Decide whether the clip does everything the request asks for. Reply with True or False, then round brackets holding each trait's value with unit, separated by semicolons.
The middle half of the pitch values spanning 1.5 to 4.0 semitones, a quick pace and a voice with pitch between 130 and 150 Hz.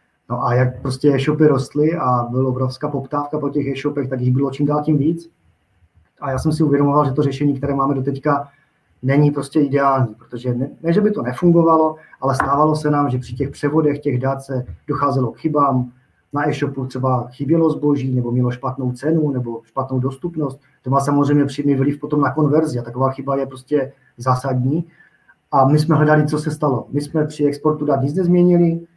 True (2.4 semitones; 200 wpm; 140 Hz)